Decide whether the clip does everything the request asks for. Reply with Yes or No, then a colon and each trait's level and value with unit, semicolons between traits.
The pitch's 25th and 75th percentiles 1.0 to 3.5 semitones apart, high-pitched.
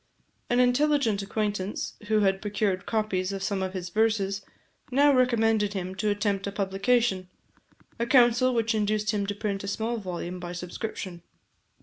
Yes: average, 2.8 semitones; high, 205 Hz